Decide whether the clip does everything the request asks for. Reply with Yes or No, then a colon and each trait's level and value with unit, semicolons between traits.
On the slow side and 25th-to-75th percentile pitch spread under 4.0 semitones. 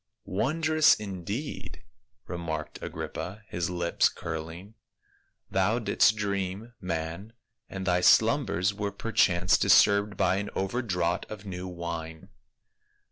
Yes: slow, 120 wpm; average, 3.3 semitones